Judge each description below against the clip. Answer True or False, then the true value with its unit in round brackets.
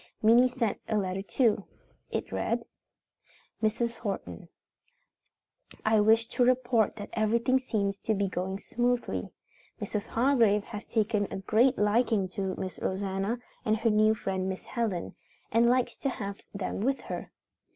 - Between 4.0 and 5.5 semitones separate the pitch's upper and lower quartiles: False (3.0 semitones)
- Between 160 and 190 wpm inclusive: False (145 wpm)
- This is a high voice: True (215 Hz)